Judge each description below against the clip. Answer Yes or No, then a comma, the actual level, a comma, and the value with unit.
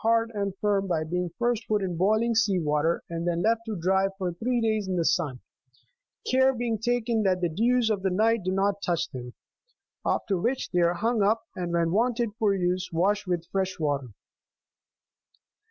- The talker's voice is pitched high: Yes, high, 195 Hz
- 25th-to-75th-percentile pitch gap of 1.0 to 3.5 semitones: No, average, 4.3 semitones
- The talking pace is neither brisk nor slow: Yes, average, 195 wpm